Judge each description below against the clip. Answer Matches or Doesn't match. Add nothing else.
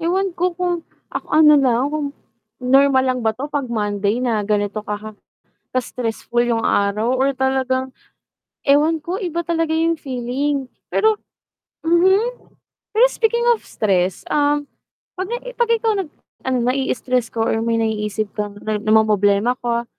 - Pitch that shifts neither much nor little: Doesn't match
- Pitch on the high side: Matches